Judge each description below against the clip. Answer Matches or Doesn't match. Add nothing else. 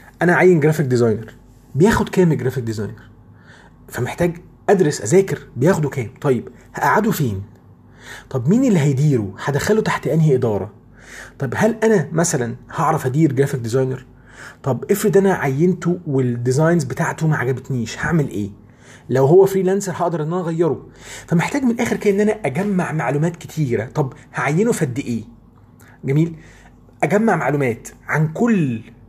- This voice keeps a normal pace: Doesn't match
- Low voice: Doesn't match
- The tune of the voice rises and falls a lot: Matches